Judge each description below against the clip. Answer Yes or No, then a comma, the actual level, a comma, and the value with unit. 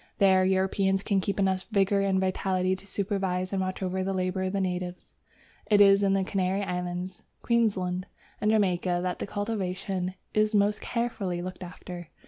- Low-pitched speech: No, high, 190 Hz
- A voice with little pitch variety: Yes, narrow, 1.5 semitones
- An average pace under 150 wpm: No, average, 165 wpm